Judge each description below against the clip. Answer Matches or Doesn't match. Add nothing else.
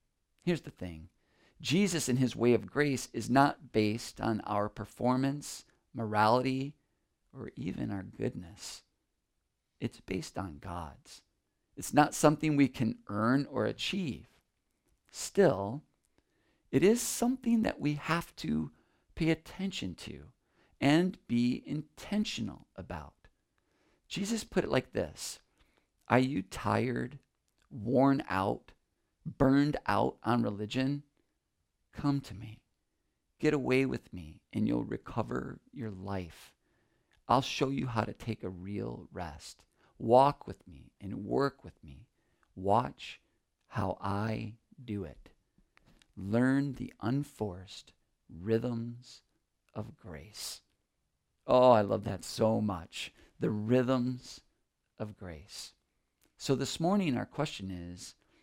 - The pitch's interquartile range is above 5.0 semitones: Matches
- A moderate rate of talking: Doesn't match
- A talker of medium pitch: Doesn't match